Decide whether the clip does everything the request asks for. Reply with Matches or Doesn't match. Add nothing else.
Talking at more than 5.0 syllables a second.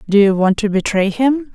Matches